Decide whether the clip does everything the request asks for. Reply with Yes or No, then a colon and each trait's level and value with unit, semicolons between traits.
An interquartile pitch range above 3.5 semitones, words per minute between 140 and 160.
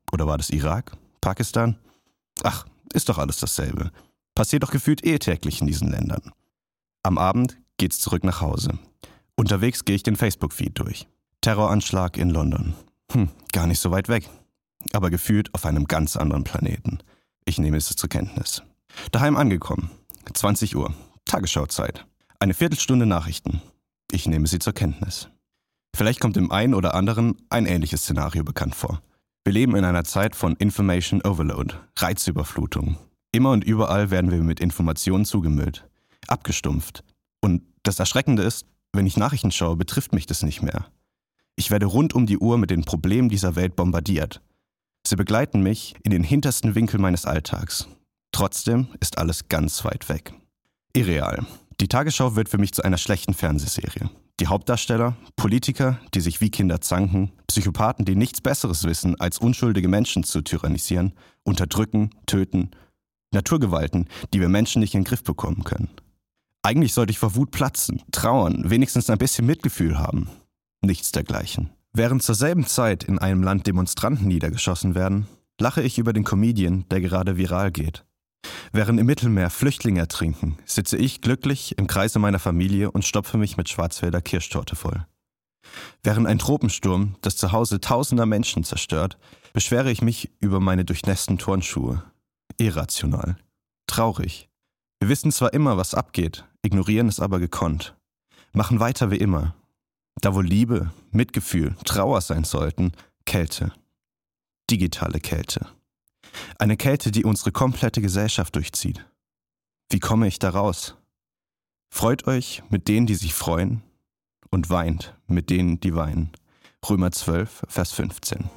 Yes: average, 4.3 semitones; average, 150 wpm